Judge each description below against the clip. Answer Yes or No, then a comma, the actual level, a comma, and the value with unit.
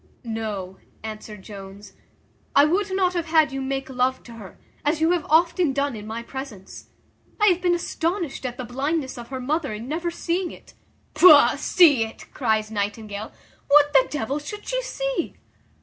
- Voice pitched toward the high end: Yes, very high, 270 Hz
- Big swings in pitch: Yes, wide, 7.1 semitones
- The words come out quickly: No, average, 175 wpm